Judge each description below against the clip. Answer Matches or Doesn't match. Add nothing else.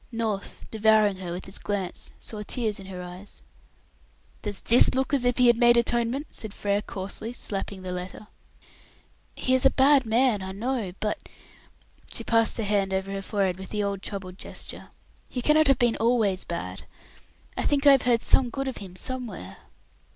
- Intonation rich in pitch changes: Doesn't match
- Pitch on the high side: Matches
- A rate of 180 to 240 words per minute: Matches